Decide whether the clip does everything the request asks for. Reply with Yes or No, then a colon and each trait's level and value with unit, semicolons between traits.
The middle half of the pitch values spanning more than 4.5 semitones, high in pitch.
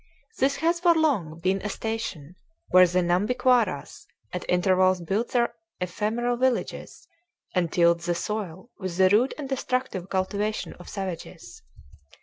Yes: average, 5.2 semitones; high, 195 Hz